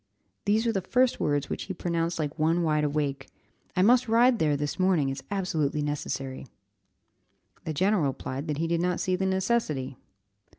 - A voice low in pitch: No, medium, 165 Hz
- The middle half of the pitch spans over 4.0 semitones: Yes, average, 4.6 semitones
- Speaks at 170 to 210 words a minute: Yes, average, 175 wpm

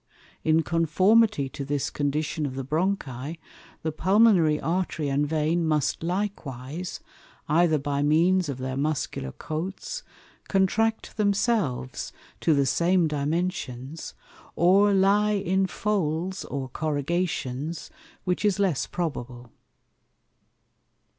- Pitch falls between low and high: Yes, medium, 160 Hz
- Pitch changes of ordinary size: Yes, average, 4.7 semitones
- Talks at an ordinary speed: No, slow, 110 wpm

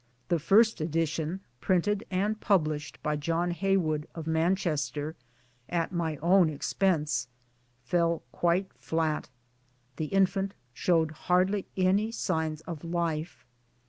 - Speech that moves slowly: Yes, slow, 110 wpm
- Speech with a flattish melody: No, average, 3.3 semitones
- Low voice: No, medium, 170 Hz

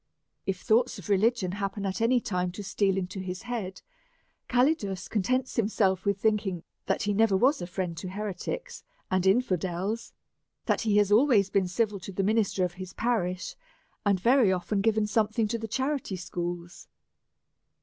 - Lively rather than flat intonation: No, average, 3.4 semitones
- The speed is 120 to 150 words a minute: No, average, 165 wpm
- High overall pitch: Yes, high, 200 Hz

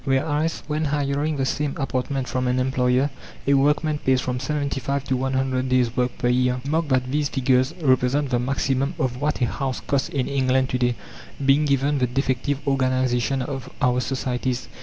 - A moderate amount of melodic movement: No, narrow, 1.9 semitones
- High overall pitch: No, low, 130 Hz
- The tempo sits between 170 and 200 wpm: Yes, average, 180 wpm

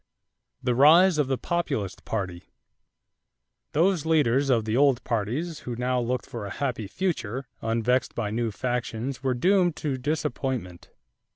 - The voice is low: Yes, low, 125 Hz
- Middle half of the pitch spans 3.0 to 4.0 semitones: No, average, 4.4 semitones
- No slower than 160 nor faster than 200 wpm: No, average, 145 wpm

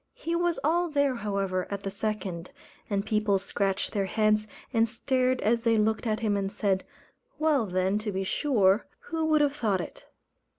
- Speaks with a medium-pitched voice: No, high, 215 Hz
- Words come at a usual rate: Yes, average, 180 wpm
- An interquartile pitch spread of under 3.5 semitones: No, average, 4.6 semitones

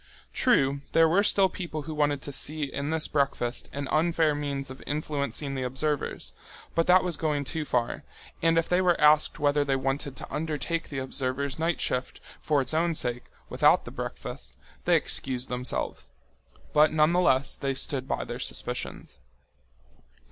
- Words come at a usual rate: Yes, average, 165 wpm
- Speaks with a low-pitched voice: No, medium, 145 Hz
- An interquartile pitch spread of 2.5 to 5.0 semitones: Yes, average, 2.9 semitones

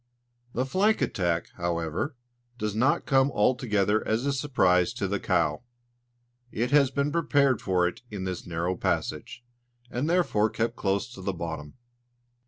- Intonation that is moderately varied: No, wide, 6.6 semitones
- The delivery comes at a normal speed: Yes, average, 150 wpm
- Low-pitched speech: Yes, low, 105 Hz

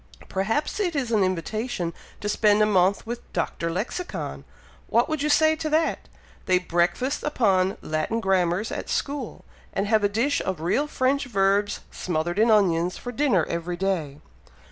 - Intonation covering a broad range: Yes, wide, 6.0 semitones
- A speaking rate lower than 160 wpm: No, average, 165 wpm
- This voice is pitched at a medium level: No, high, 205 Hz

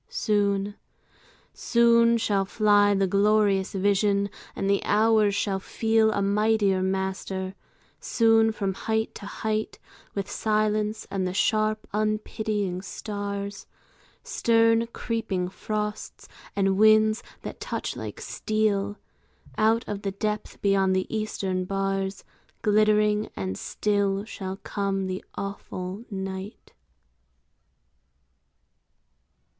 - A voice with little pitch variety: Yes, narrow, 1.8 semitones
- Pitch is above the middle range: Yes, high, 205 Hz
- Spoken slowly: Yes, slow, 105 wpm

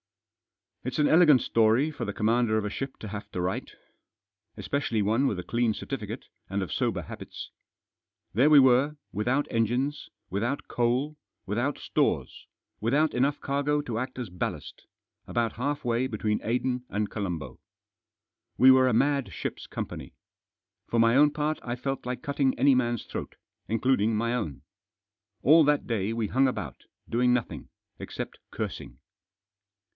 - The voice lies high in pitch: No, low, 125 Hz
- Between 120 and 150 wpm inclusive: No, average, 160 wpm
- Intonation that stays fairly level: No, average, 4.0 semitones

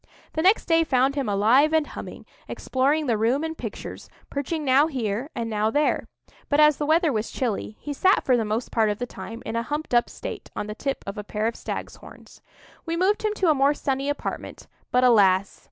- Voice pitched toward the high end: Yes, very high, 265 Hz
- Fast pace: Yes, fast, 220 wpm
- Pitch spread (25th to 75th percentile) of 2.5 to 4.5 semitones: No, average, 5.2 semitones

